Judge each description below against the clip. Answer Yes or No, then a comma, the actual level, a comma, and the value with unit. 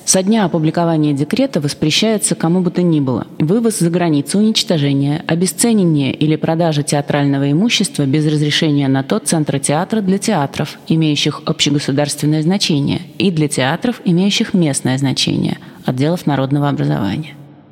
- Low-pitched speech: No, medium, 155 Hz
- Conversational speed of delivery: Yes, average, 130 wpm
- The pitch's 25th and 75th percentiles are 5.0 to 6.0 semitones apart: No, average, 3.9 semitones